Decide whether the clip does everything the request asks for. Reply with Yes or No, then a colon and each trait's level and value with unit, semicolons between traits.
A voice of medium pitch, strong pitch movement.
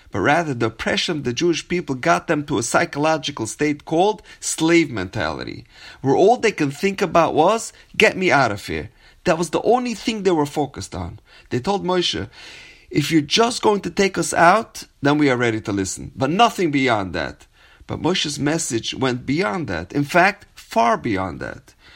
Yes: medium, 160 Hz; wide, 6.0 semitones